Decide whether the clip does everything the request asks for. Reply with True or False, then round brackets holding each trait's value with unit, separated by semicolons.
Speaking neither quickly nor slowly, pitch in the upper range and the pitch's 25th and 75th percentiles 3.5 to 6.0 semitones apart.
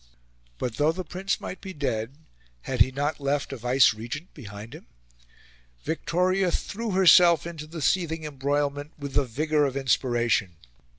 False (150 wpm; 145 Hz; 4.6 semitones)